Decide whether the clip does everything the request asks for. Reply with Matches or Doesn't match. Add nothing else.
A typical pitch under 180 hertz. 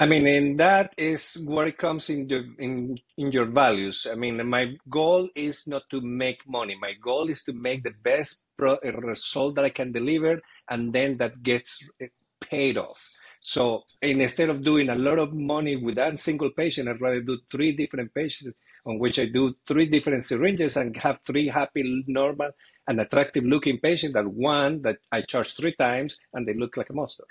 Matches